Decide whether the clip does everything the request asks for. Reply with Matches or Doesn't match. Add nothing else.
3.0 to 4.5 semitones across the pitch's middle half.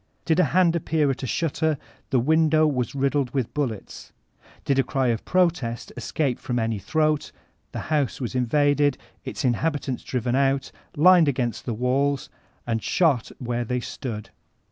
Matches